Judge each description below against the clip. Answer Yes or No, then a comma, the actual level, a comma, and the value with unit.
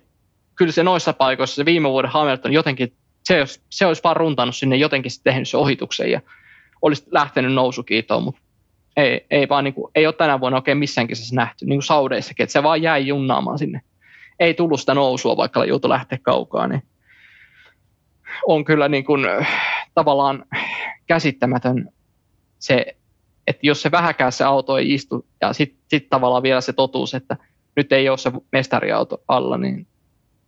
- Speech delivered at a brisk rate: Yes, fast, 165 wpm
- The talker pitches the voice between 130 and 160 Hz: Yes, low, 135 Hz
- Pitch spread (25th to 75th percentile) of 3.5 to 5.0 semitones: No, average, 2.8 semitones